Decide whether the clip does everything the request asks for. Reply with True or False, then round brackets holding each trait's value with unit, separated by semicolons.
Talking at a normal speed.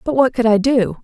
False (290 wpm)